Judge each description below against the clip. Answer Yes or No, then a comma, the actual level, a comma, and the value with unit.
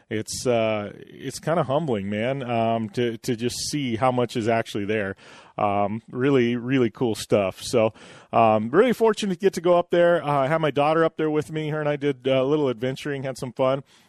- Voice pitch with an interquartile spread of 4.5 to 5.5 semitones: Yes, average, 4.9 semitones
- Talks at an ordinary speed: No, fast, 220 wpm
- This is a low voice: Yes, low, 130 Hz